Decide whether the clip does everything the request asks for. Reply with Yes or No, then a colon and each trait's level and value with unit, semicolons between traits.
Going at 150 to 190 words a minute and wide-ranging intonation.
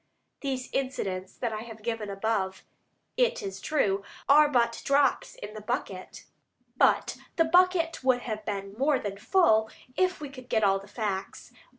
Yes: average, 155 wpm; wide, 6.1 semitones